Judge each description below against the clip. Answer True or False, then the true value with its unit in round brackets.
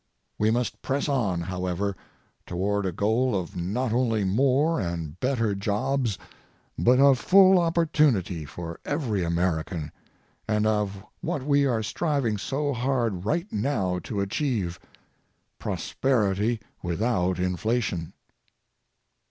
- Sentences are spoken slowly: True (115 wpm)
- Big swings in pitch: True (6.3 semitones)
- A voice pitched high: False (110 Hz)